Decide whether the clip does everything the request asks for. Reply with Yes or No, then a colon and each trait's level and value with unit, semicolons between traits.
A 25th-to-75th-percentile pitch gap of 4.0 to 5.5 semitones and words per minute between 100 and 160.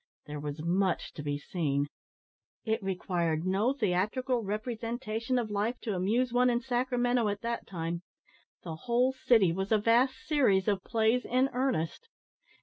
Yes: average, 5.2 semitones; average, 150 wpm